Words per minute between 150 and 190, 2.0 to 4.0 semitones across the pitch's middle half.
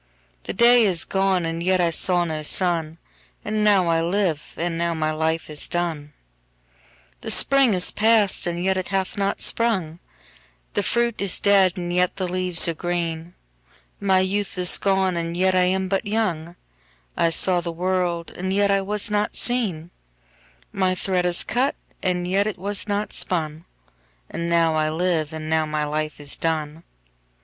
Yes: average, 160 wpm; average, 3.4 semitones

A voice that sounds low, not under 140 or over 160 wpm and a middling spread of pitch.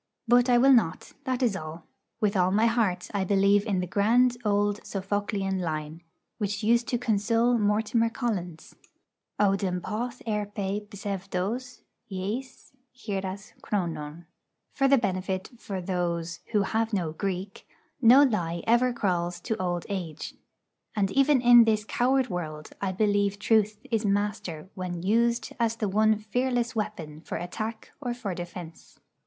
No: high, 205 Hz; average, 145 wpm; average, 3.8 semitones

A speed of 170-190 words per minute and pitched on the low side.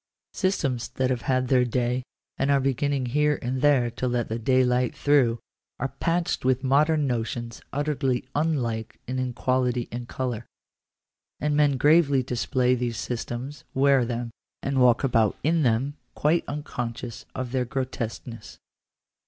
No: average, 145 wpm; low, 130 Hz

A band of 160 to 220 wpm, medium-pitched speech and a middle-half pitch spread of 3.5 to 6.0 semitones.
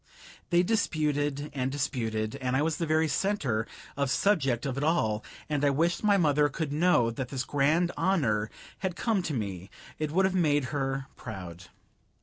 Yes: average, 175 wpm; medium, 145 Hz; average, 4.6 semitones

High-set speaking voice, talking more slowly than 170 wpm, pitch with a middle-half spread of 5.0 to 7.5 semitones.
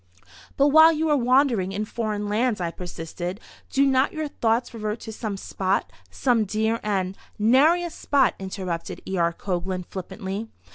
Yes: high, 215 Hz; average, 155 wpm; wide, 5.4 semitones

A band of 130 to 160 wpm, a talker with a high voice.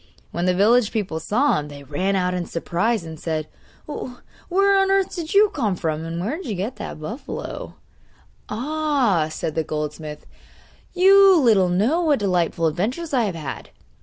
No: average, 170 wpm; high, 205 Hz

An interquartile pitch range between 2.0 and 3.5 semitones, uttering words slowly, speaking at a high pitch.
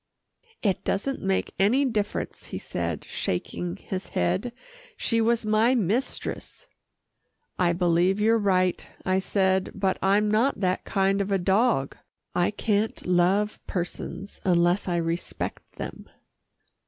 Yes: average, 3.0 semitones; slow, 130 wpm; high, 195 Hz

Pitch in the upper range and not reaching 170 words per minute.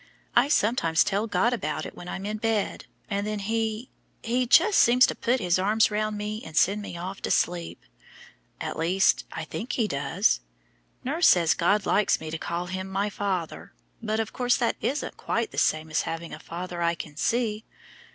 No: high, 205 Hz; average, 195 wpm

